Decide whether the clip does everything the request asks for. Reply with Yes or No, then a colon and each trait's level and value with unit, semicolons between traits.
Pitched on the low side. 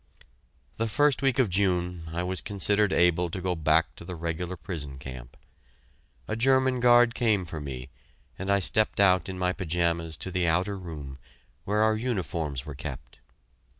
Yes: very low, 90 Hz